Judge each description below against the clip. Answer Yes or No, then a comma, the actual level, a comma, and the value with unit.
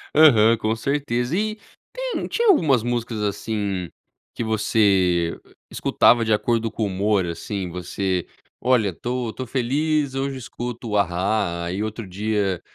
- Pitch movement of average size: Yes, average, 4.3 semitones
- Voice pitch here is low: Yes, low, 110 Hz